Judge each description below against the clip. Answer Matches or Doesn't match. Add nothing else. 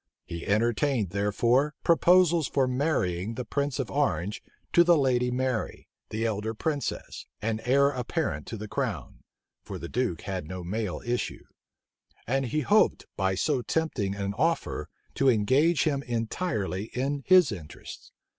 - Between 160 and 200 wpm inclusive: Doesn't match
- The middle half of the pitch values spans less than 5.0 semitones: Doesn't match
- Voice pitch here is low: Matches